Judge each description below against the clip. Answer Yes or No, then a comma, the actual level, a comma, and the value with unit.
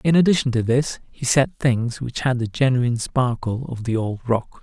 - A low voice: Yes, low, 125 Hz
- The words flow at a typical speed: No, fast, 210 wpm